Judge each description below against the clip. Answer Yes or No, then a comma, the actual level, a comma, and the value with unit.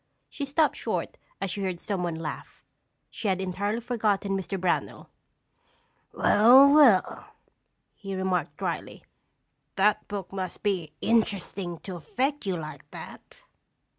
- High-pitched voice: Yes, high, 195 Hz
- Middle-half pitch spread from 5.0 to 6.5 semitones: No, average, 3.3 semitones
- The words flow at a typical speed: No, slow, 125 wpm